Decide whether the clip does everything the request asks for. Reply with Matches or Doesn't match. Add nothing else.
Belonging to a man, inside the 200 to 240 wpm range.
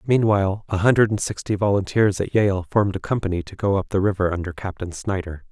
Matches